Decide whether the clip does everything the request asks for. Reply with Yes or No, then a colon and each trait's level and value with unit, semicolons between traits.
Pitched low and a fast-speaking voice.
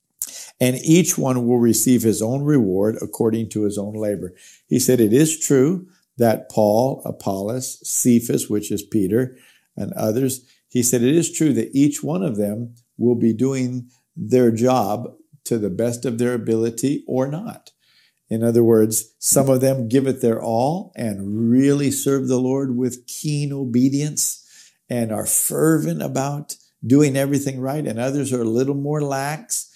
No: low, 125 Hz; average, 165 wpm